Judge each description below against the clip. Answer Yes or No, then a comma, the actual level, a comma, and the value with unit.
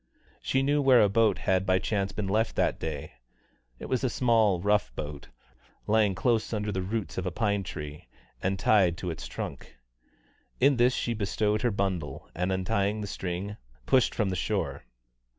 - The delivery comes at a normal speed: Yes, average, 180 wpm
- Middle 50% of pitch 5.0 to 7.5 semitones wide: No, average, 3.3 semitones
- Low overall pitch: Yes, low, 100 Hz